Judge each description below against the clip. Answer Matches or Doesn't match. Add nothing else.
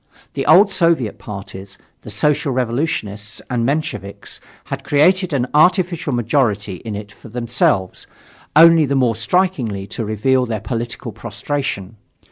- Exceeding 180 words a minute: Doesn't match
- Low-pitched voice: Matches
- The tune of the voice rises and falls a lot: Matches